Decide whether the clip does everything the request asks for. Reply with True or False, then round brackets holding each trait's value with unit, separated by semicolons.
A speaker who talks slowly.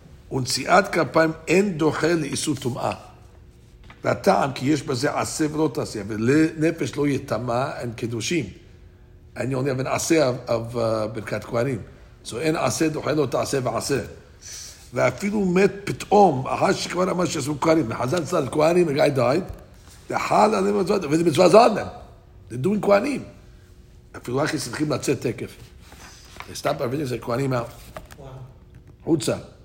True (130 wpm)